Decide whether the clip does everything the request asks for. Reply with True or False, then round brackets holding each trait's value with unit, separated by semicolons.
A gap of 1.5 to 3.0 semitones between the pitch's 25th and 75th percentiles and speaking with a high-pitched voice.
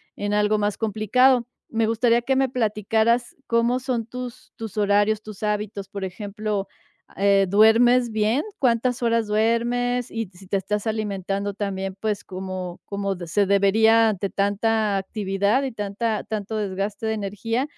True (2.6 semitones; 215 Hz)